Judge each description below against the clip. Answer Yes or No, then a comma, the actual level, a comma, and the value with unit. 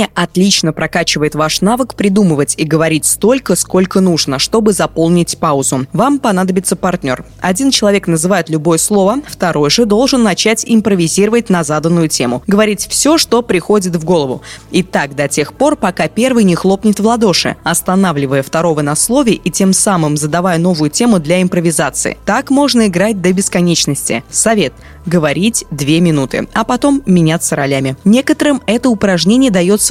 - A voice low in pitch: No, medium, 185 Hz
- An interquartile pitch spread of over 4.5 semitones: Yes, average, 5.2 semitones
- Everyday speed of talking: Yes, average, 150 wpm